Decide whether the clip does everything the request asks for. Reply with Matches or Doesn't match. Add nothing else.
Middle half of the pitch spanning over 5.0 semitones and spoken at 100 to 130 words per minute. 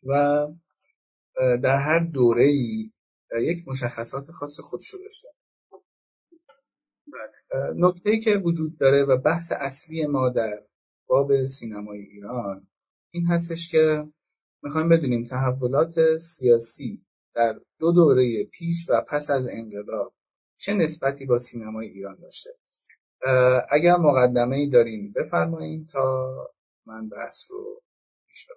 Matches